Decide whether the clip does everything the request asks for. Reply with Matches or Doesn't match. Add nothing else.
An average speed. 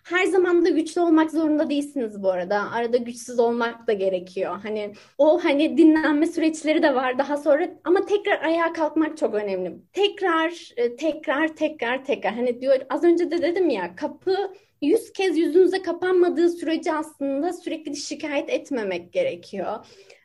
Doesn't match